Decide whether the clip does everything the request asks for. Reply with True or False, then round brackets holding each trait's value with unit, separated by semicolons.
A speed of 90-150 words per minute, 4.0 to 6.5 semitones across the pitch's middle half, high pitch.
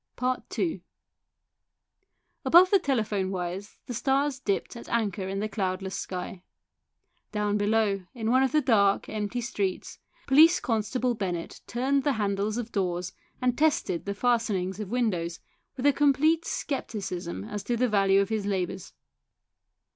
True (145 wpm; 4.5 semitones; 215 Hz)